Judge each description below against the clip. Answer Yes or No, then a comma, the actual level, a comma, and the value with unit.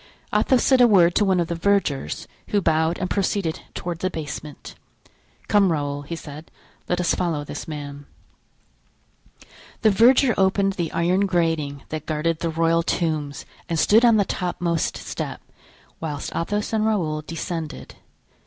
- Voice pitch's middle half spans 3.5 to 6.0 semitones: Yes, average, 4.1 semitones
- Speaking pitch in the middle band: Yes, medium, 170 Hz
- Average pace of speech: Yes, average, 155 wpm